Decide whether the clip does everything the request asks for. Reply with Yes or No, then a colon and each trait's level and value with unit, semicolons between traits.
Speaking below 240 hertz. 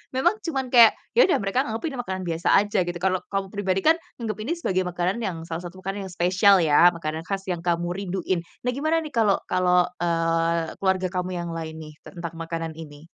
Yes: medium, 185 Hz